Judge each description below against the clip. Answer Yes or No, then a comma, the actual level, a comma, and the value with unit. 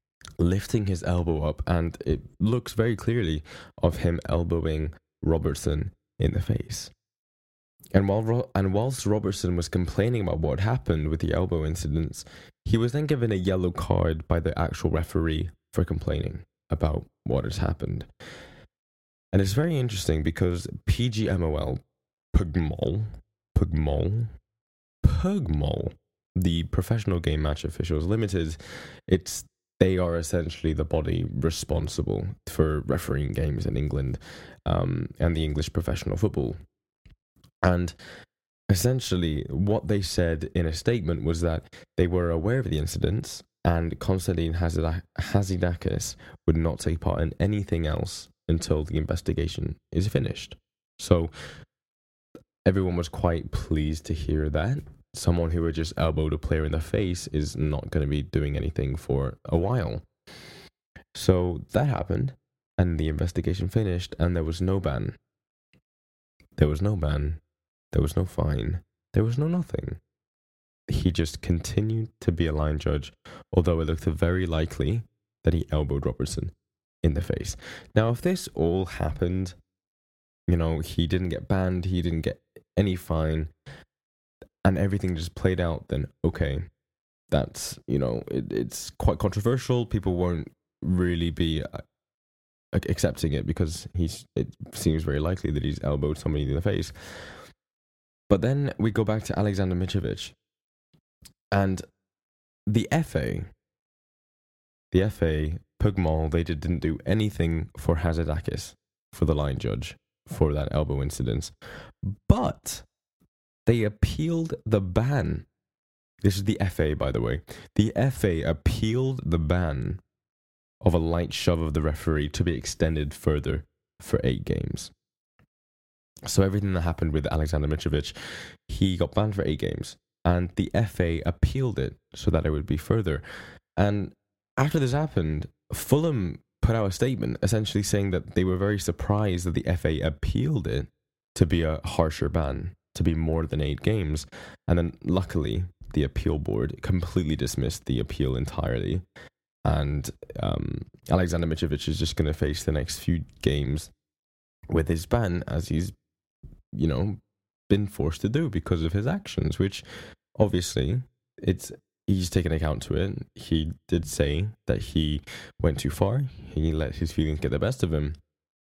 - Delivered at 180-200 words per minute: No, average, 145 wpm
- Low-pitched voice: Yes, very low, 85 Hz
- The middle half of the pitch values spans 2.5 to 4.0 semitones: No, average, 4.4 semitones